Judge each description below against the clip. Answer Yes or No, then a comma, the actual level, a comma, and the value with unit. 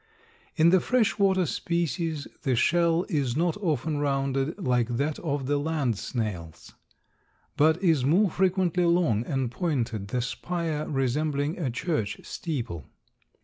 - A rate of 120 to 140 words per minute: Yes, slow, 135 wpm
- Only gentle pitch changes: No, average, 5.0 semitones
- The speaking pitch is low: No, medium, 150 Hz